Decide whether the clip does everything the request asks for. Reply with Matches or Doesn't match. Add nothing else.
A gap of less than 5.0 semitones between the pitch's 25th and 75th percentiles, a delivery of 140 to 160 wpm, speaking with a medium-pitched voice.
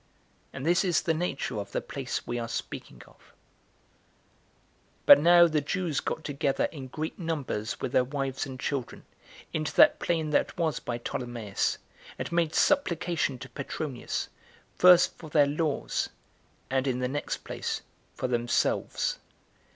Matches